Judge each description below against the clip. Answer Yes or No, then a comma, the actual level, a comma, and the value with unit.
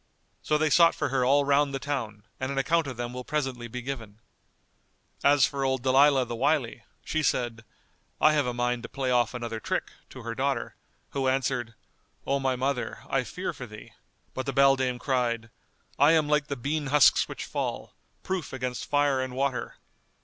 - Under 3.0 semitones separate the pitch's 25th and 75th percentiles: Yes, narrow, 2.5 semitones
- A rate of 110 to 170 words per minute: No, average, 190 wpm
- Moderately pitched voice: No, low, 130 Hz